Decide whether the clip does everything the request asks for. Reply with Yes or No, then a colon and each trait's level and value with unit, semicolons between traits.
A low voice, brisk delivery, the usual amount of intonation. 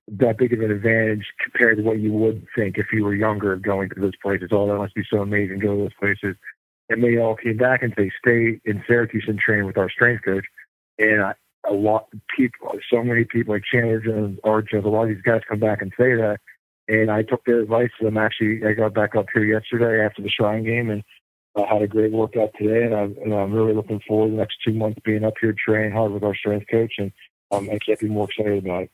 No: low, 110 Hz; fast, 255 wpm; narrow, 1.3 semitones